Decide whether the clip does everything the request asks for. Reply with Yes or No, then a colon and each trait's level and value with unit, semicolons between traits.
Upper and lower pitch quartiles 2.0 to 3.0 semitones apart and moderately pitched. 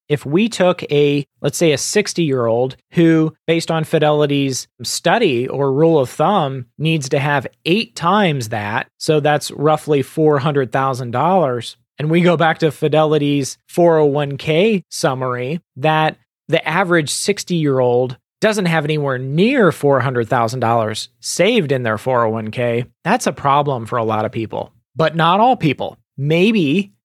No: average, 4.4 semitones; medium, 150 Hz